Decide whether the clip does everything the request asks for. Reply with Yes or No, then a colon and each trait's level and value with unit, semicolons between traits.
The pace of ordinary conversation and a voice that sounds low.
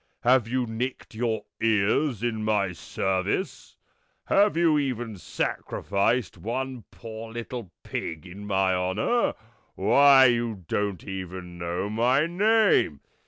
No: slow, 115 wpm; low, 110 Hz